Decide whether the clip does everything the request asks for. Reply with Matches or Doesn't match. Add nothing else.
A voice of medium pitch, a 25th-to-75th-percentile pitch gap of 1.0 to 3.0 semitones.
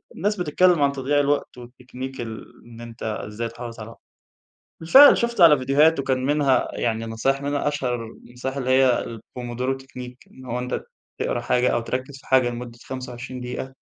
Doesn't match